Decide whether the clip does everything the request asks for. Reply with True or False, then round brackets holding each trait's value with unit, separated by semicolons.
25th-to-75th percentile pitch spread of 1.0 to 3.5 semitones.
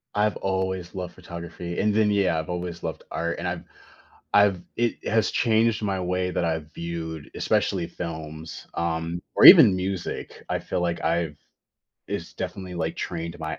True (2.5 semitones)